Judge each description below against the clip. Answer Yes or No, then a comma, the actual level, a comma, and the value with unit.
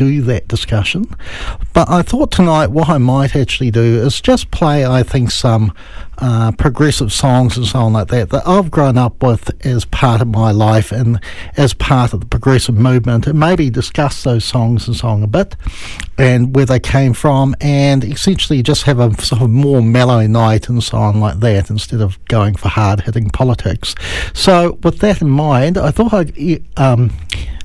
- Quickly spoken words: No, average, 190 wpm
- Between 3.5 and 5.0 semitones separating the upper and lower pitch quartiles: Yes, average, 3.9 semitones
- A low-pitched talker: Yes, low, 125 Hz